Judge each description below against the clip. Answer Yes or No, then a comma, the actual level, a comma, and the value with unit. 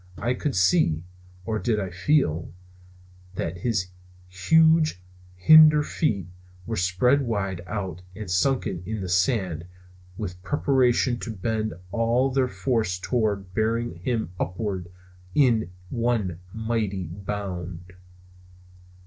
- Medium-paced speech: No, slow, 115 wpm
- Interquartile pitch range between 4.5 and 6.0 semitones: Yes, average, 4.9 semitones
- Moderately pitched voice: No, low, 105 Hz